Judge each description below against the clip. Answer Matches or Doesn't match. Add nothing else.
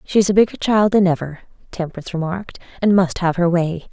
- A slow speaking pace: Doesn't match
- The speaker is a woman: Matches